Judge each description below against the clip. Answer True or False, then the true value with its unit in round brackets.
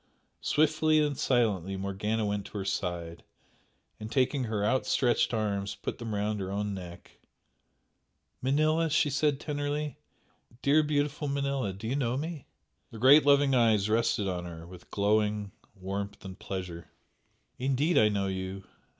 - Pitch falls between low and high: False (110 Hz)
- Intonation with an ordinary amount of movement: False (6.3 semitones)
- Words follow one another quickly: False (145 wpm)